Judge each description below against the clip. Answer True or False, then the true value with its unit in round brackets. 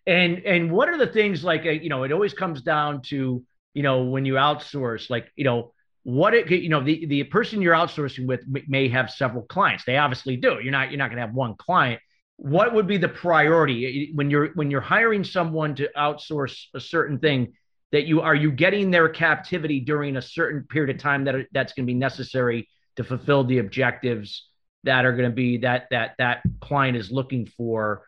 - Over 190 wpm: True (205 wpm)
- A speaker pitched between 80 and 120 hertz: False (140 Hz)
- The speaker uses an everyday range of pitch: True (3.7 semitones)